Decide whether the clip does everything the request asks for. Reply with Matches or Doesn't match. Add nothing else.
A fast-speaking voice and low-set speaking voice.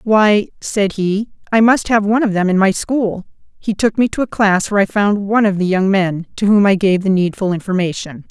Doesn't match